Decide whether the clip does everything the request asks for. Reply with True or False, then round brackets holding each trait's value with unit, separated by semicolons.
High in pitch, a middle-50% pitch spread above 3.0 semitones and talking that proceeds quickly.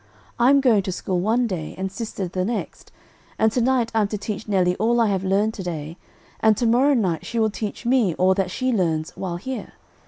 True (210 Hz; 4.1 semitones; 220 wpm)